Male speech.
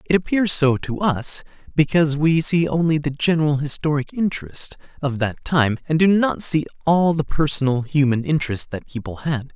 Yes: male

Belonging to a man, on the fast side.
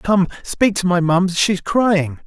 Yes: male; fast, 210 wpm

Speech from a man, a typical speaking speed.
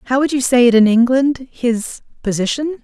No: female; average, 170 wpm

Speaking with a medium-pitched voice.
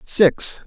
Yes: medium, 175 Hz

